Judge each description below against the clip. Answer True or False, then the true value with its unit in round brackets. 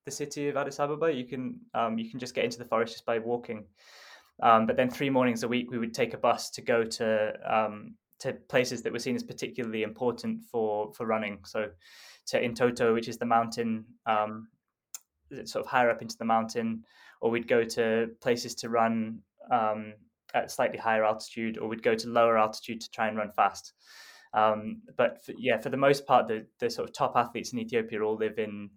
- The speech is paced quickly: True (215 wpm)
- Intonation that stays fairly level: True (2.3 semitones)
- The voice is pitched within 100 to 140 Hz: True (115 Hz)